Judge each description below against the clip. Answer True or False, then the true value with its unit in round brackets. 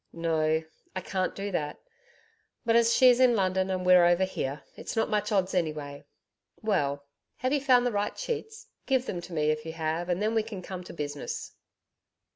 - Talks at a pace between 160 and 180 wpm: False (195 wpm)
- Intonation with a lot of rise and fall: True (5.7 semitones)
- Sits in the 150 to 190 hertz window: True (185 Hz)